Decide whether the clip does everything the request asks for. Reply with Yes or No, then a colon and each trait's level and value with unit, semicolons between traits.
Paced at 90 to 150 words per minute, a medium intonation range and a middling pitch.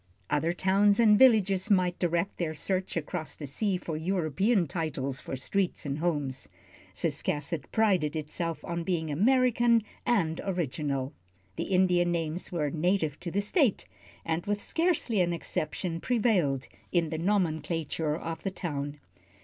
Yes: average, 140 wpm; average, 4.2 semitones; medium, 175 Hz